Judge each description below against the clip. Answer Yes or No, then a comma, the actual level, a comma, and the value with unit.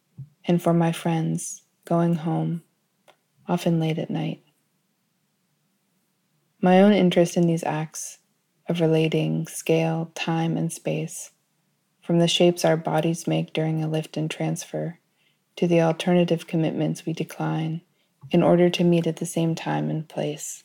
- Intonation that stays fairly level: Yes, narrow, 1.8 semitones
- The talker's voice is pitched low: No, medium, 165 Hz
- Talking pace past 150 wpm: No, average, 140 wpm